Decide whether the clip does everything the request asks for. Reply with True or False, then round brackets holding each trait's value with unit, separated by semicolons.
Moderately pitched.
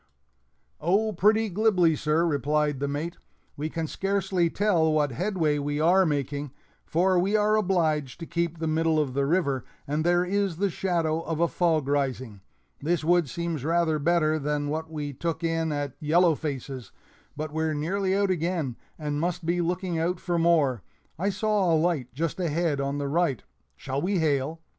True (160 Hz)